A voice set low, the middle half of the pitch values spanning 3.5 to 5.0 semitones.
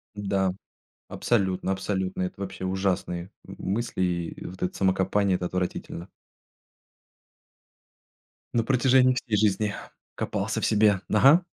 No: very low, 95 Hz; narrow, 2.6 semitones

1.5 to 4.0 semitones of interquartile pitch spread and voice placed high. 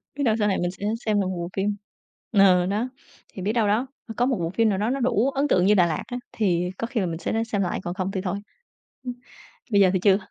Yes: average, 3.6 semitones; high, 205 Hz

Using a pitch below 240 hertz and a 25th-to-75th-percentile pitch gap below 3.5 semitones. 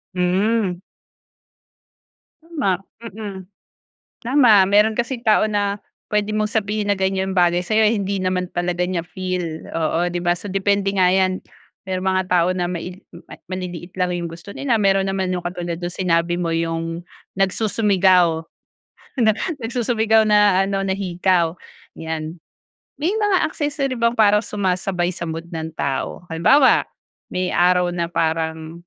Yes: medium, 185 Hz; average, 3.1 semitones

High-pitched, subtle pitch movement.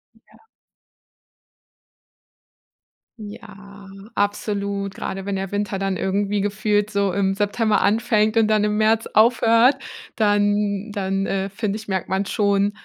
Yes: high, 205 Hz; narrow, 1.4 semitones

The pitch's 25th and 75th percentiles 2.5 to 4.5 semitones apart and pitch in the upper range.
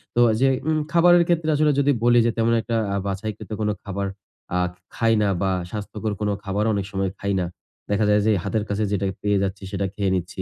No: average, 2.9 semitones; low, 105 Hz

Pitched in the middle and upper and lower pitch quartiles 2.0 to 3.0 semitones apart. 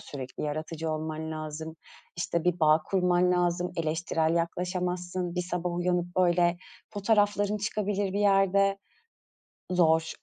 Yes: medium, 175 Hz; narrow, 2.4 semitones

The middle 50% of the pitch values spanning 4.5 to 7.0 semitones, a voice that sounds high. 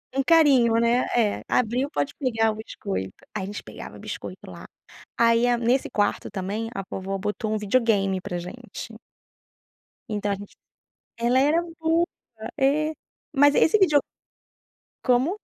Yes: average, 4.8 semitones; high, 235 Hz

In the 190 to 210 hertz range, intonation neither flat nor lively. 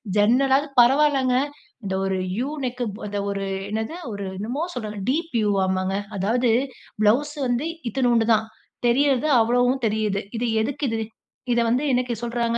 No: high, 240 Hz; average, 3.6 semitones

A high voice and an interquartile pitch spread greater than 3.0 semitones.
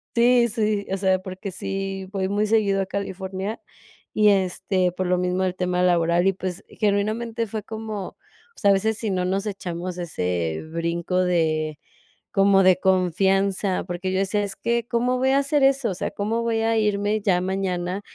No: high, 195 Hz; average, 2.7 semitones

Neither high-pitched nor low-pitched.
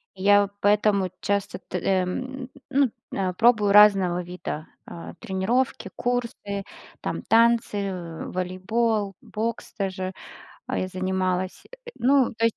No: high, 200 Hz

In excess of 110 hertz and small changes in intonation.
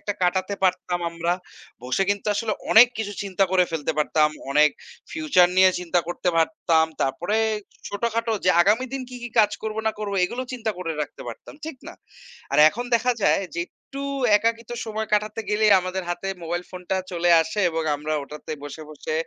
No: high, 190 Hz; average, 4.7 semitones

